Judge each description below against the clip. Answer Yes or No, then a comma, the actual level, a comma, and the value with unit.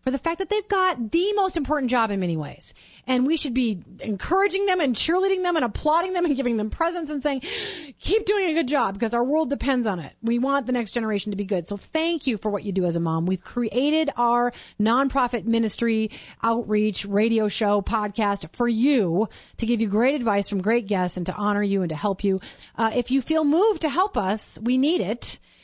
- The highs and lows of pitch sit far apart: Yes, wide, 6.8 semitones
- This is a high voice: Yes, high, 240 Hz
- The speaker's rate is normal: No, fast, 230 wpm